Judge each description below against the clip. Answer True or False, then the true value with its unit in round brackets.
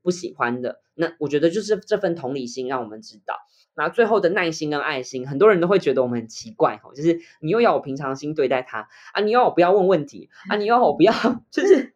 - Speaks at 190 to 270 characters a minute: False (365 characters per minute)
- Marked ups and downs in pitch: True (8.4 semitones)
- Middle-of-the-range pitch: True (165 Hz)